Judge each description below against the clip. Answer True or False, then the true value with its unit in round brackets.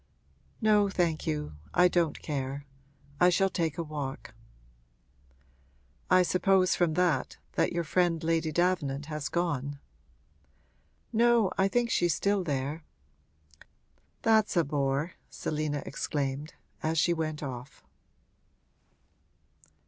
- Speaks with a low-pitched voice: False (160 Hz)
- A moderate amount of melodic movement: True (4.0 semitones)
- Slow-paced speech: True (115 wpm)